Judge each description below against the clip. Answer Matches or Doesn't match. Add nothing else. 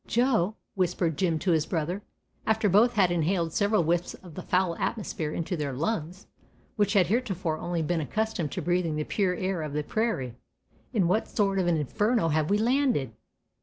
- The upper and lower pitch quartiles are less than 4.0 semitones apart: Doesn't match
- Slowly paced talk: Doesn't match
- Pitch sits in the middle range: Matches